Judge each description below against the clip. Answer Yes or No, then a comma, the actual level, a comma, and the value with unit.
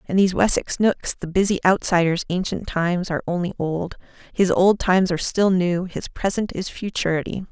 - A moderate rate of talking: Yes, average, 175 wpm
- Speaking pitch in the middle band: Yes, medium, 180 Hz